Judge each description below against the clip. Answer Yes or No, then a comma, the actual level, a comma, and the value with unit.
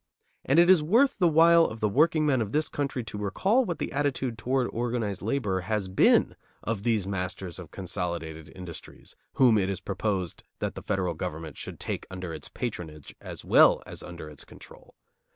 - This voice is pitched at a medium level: No, low, 105 Hz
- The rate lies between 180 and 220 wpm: Yes, average, 185 wpm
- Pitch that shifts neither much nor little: No, wide, 7.2 semitones